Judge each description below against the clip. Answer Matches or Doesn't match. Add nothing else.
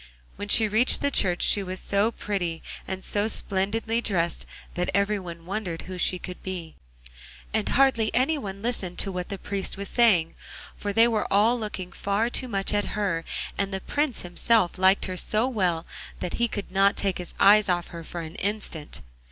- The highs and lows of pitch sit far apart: Doesn't match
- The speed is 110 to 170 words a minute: Doesn't match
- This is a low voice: Doesn't match